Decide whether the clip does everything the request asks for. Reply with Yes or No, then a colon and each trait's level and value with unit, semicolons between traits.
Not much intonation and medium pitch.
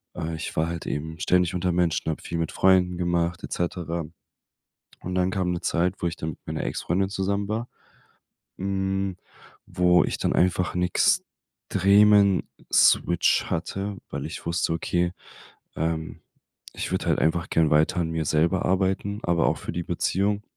No: narrow, 2.3 semitones; very low, 90 Hz